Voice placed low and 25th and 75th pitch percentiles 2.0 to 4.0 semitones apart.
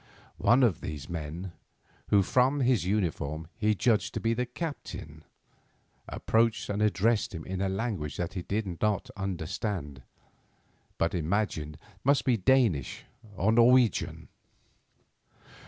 No: low, 100 Hz; wide, 5.4 semitones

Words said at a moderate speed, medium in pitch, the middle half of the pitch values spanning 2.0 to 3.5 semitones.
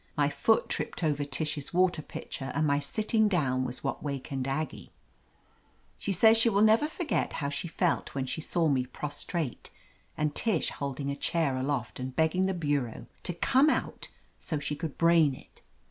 No: average, 175 wpm; medium, 150 Hz; average, 4.4 semitones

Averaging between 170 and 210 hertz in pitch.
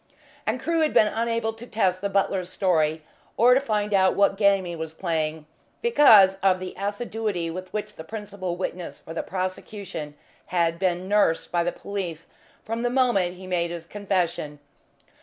Yes: high, 190 Hz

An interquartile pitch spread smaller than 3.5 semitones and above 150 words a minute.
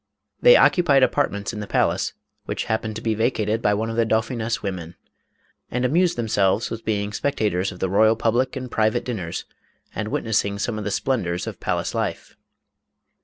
Yes: average, 2.8 semitones; average, 175 wpm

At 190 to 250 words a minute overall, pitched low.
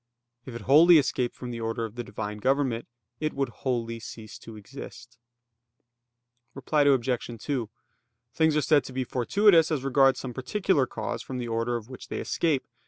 No: average, 175 wpm; low, 130 Hz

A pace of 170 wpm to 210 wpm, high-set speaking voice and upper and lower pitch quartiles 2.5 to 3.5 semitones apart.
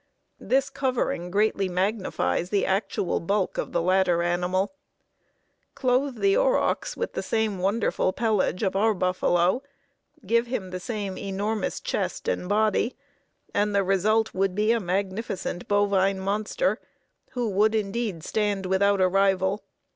No: slow, 135 wpm; high, 200 Hz; average, 2.8 semitones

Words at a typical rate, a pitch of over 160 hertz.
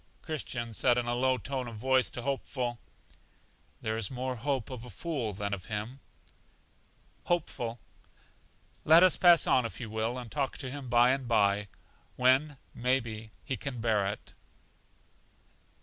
No: average, 160 wpm; low, 125 Hz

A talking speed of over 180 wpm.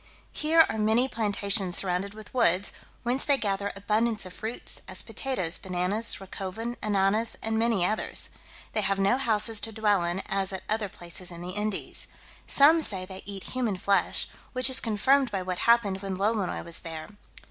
No: average, 175 wpm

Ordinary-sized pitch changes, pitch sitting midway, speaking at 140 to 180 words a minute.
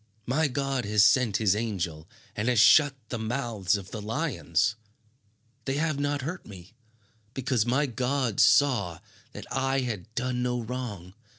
No: average, 4.4 semitones; low, 120 Hz; average, 155 wpm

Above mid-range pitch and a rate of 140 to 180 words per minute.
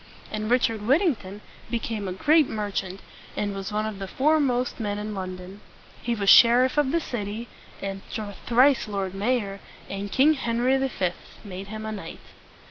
Yes: high, 215 Hz; average, 160 wpm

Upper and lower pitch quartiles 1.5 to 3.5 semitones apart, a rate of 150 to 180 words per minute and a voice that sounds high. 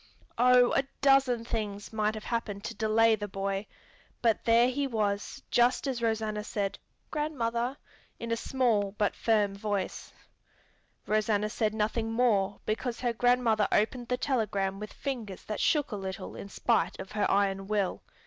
Yes: average, 2.8 semitones; average, 160 wpm; high, 220 Hz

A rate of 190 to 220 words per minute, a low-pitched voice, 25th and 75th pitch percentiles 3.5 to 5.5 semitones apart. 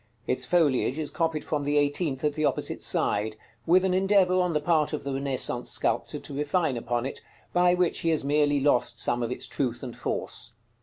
No: fast, 205 wpm; medium, 145 Hz; average, 4.0 semitones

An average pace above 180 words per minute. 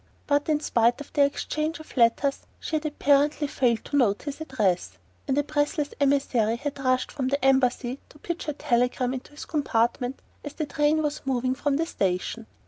Yes: average, 190 wpm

